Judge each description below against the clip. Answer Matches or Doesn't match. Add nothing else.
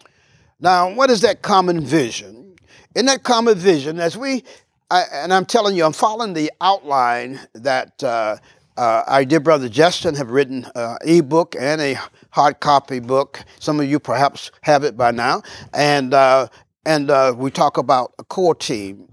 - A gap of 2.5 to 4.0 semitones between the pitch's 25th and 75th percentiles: Doesn't match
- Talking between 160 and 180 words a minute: Matches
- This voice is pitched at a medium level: Matches